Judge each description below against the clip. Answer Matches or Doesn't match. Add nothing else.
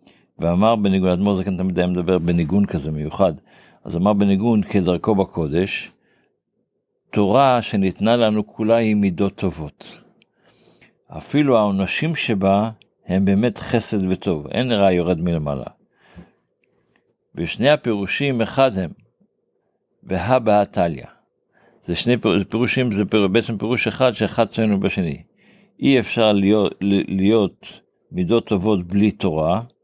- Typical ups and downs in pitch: Matches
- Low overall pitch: Matches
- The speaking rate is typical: Matches